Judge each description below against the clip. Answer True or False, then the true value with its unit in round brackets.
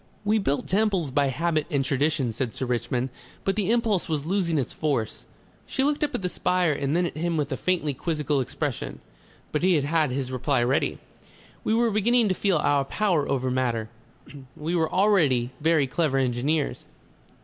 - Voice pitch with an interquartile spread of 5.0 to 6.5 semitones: True (5.4 semitones)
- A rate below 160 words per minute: False (180 wpm)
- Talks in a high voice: False (155 Hz)